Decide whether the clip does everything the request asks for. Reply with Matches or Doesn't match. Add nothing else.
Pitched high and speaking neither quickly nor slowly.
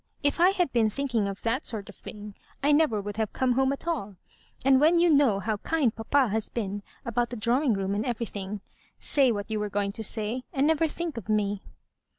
Doesn't match